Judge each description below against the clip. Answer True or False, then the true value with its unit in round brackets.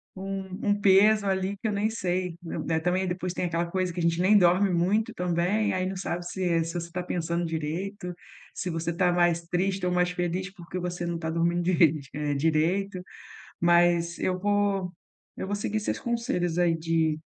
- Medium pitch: True (180 Hz)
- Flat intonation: True (2.0 semitones)